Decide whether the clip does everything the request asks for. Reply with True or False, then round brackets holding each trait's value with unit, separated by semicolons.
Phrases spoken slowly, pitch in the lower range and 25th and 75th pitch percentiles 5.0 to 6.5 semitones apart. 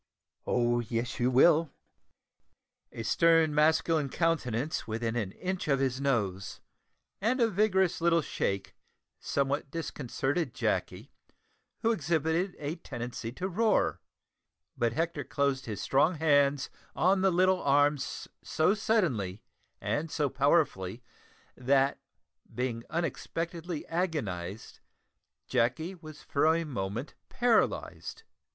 False (110 wpm; 145 Hz; 5.5 semitones)